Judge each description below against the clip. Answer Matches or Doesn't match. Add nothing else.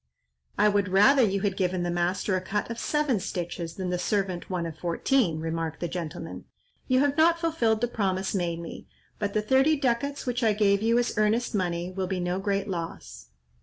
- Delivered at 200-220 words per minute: Matches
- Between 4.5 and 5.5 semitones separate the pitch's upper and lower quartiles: Matches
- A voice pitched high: Matches